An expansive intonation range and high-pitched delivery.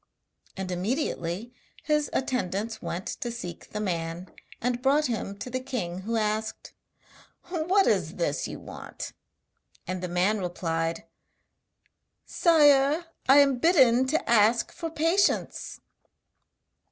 Yes: wide, 7.5 semitones; high, 235 Hz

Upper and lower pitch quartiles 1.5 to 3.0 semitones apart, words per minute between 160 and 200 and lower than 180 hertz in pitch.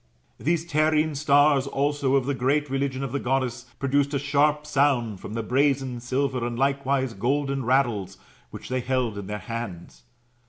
Yes: average, 2.7 semitones; average, 165 wpm; low, 135 Hz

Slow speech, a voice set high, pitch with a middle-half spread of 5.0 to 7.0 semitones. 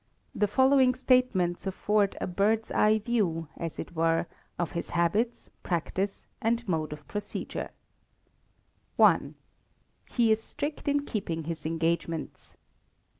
Yes: slow, 125 wpm; high, 200 Hz; wide, 5.5 semitones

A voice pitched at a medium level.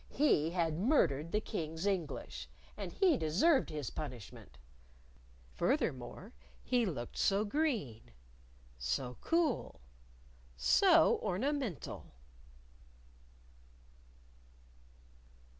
Yes: medium, 175 Hz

